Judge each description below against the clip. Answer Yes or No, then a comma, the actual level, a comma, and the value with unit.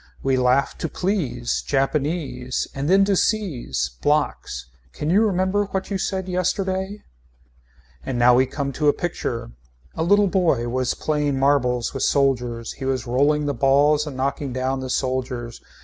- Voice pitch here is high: No, medium, 140 Hz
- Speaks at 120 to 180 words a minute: Yes, average, 160 wpm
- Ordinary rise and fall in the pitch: No, wide, 5.7 semitones